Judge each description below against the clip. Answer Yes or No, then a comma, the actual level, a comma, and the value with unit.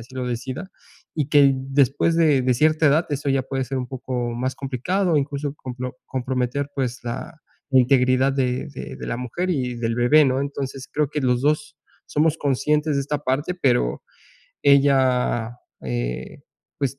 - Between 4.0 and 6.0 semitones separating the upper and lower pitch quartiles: No, narrow, 2.6 semitones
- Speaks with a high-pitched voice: No, low, 135 Hz